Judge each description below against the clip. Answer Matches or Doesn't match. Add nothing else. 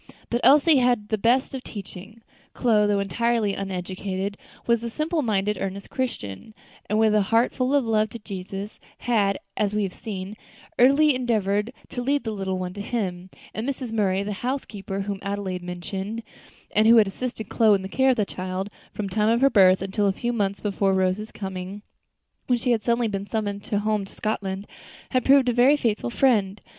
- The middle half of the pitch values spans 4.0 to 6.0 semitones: Doesn't match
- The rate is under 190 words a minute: Doesn't match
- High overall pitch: Matches